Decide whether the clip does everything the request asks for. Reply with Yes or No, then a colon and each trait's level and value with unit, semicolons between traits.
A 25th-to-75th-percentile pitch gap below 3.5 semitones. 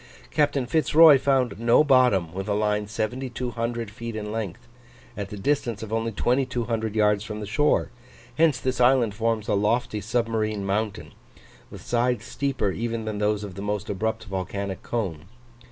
Yes: average, 2.9 semitones